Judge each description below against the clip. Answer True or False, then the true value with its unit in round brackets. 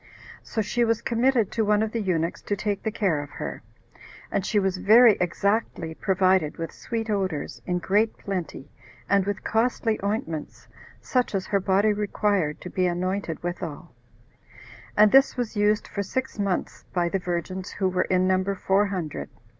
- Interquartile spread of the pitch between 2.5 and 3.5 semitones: True (2.8 semitones)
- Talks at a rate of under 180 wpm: True (170 wpm)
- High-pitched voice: True (195 Hz)